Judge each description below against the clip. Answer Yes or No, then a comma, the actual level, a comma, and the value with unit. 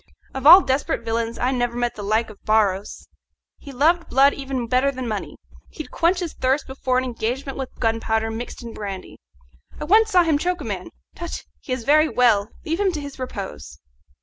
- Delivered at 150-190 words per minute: No, average, 200 wpm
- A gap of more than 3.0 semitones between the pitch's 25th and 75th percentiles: Yes, average, 4.7 semitones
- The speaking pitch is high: Yes, very high, 255 Hz